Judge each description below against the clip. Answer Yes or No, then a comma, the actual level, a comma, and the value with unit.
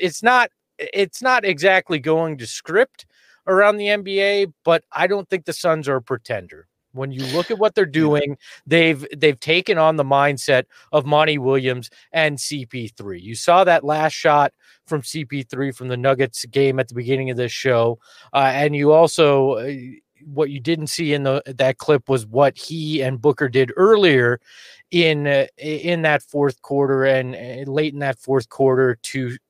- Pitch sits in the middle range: Yes, medium, 145 Hz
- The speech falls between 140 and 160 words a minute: No, average, 185 wpm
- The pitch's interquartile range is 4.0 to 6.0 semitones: No, average, 3.6 semitones